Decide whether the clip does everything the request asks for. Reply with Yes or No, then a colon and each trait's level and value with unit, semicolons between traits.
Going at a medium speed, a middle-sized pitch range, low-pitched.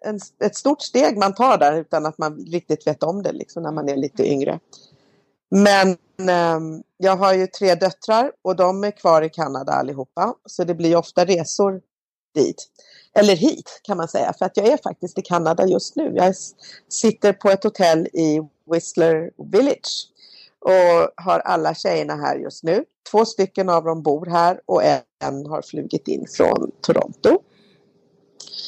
No: average, 170 wpm; average, 3.3 semitones; medium, 180 Hz